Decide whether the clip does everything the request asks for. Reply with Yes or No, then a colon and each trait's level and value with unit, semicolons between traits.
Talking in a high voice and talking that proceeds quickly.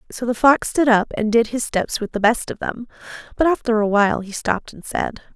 Yes: high, 230 Hz; fast, 245 wpm